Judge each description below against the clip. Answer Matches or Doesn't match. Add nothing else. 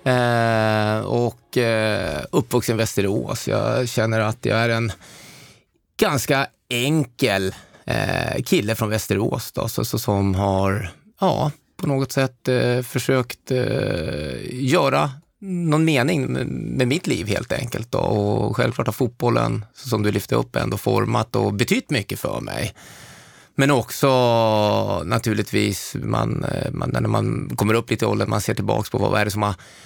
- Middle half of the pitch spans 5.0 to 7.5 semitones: Doesn't match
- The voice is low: Matches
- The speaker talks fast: Doesn't match